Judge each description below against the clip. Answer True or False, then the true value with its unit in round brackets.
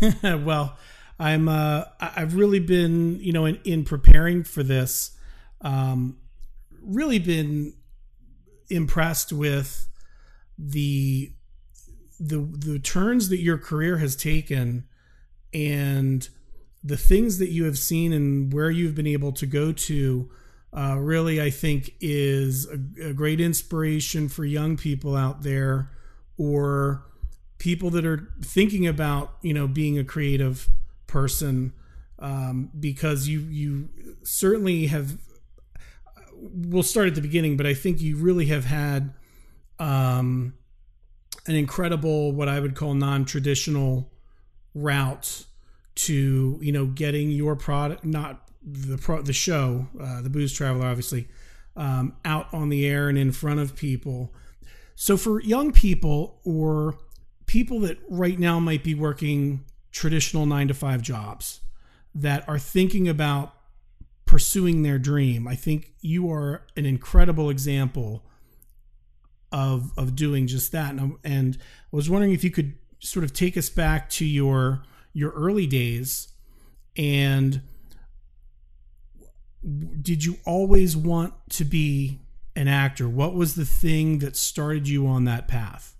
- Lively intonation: False (3.2 semitones)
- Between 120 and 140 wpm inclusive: True (135 wpm)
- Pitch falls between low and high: True (145 Hz)